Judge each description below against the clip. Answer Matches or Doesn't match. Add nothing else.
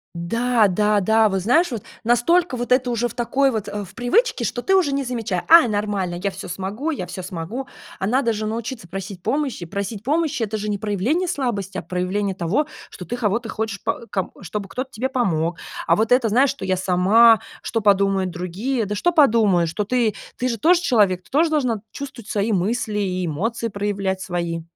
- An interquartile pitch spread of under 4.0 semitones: Doesn't match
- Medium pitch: Doesn't match